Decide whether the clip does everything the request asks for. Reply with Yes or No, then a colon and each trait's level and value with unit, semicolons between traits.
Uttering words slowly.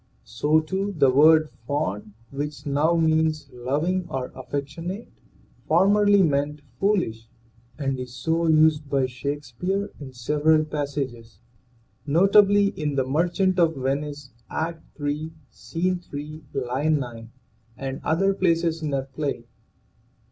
Yes: slow, 125 wpm